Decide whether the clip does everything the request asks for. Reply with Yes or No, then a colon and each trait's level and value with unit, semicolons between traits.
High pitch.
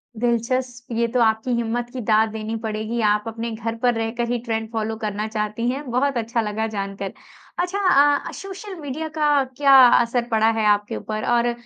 Yes: high, 230 Hz